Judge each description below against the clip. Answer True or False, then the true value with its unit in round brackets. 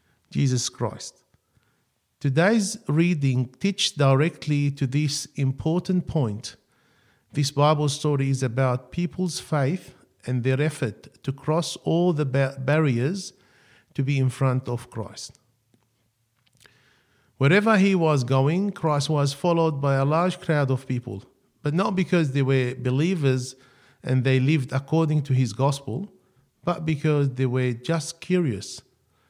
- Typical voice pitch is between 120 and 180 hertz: True (140 Hz)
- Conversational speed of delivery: False (130 wpm)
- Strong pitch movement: False (3.7 semitones)